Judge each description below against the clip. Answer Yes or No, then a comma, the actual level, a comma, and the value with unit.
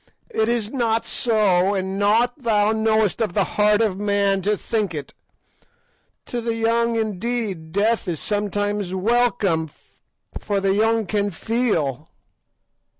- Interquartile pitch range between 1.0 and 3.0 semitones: Yes, average, 2.7 semitones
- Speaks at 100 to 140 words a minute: Yes, slow, 135 wpm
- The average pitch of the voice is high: Yes, high, 210 Hz